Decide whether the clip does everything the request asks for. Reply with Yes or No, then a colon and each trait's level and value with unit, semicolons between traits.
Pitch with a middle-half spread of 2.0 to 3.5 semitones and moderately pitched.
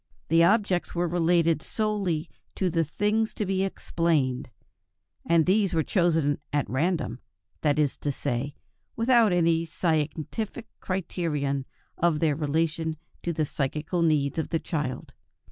Yes: average, 3.2 semitones; medium, 165 Hz